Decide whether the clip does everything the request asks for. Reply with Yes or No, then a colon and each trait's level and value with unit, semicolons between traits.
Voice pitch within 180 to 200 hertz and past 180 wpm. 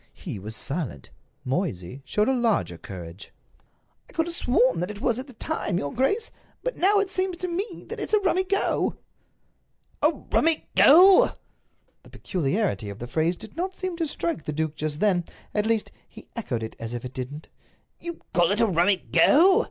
No: high, 210 Hz; average, 190 wpm